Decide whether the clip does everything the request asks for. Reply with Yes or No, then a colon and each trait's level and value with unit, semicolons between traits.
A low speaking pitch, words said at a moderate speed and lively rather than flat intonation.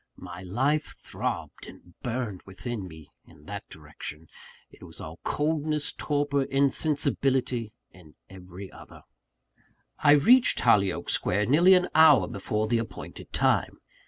No: low, 120 Hz; slow, 130 wpm; wide, 7.7 semitones